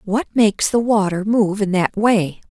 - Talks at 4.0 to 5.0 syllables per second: Yes, 4.5 syllables/s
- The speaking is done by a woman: Yes, female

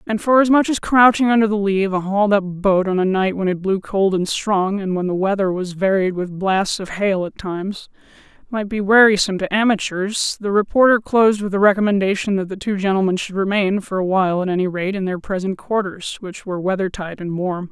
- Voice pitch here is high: Yes, high, 195 Hz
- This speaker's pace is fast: Yes, fast, 225 wpm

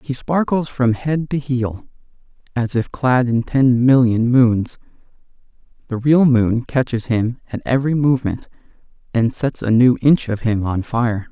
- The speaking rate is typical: Yes, average, 160 wpm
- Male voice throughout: Yes, male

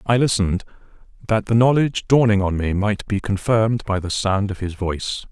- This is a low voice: Yes, low, 105 Hz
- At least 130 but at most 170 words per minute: No, average, 190 wpm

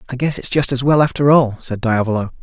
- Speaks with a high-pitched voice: No, low, 130 Hz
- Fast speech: Yes, fast, 250 wpm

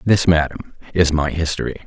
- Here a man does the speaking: Yes, male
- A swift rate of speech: No, average, 160 wpm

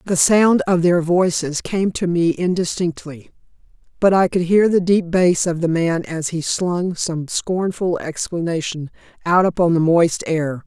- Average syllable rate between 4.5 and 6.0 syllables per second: No, 4.1 syllables/s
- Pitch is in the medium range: Yes, medium, 175 Hz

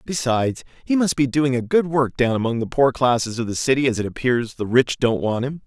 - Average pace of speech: No, fast, 255 wpm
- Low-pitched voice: Yes, low, 130 Hz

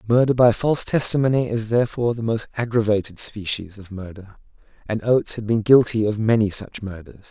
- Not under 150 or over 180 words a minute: Yes, average, 175 wpm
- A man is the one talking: Yes, male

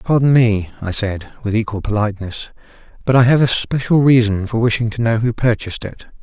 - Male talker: Yes, male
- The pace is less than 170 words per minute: No, average, 195 wpm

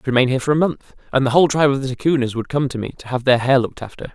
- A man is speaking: Yes, male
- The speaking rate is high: Yes, fast, 345 wpm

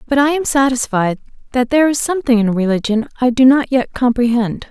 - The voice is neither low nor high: No, very high, 250 Hz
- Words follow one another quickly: No, average, 190 wpm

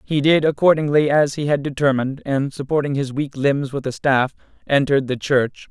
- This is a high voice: No, medium, 140 Hz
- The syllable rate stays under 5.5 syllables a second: Yes, 5.3 syllables/s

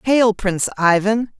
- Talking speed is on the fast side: No, slow, 130 wpm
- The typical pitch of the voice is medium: No, high, 210 Hz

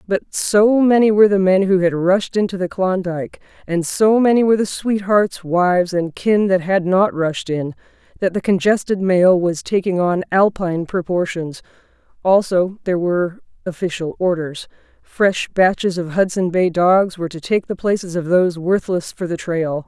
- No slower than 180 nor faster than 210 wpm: No, average, 170 wpm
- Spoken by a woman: Yes, female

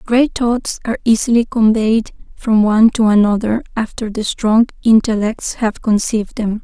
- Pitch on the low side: No, high, 220 Hz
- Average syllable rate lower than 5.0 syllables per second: Yes, 4.8 syllables/s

